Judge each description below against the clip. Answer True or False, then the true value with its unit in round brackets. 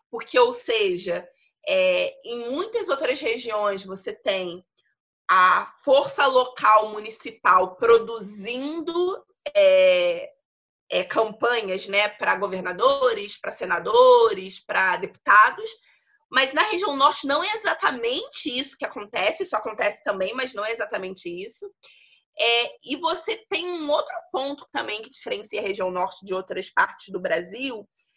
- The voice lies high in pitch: True (275 Hz)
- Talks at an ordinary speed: False (130 wpm)